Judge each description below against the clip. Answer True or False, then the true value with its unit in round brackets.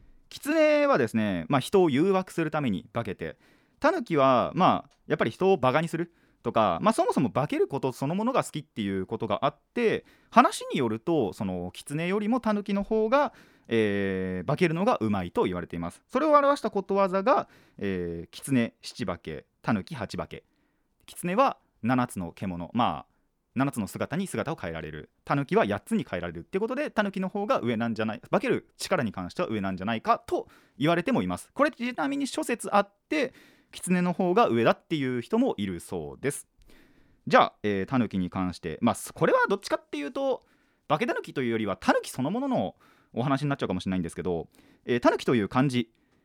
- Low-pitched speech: False (145 Hz)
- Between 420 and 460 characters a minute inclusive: False (390 characters per minute)